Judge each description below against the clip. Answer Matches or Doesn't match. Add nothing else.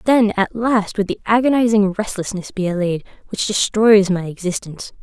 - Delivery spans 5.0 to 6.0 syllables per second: Matches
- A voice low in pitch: Doesn't match